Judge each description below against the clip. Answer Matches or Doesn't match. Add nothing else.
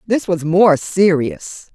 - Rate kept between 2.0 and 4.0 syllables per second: Matches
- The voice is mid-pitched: Matches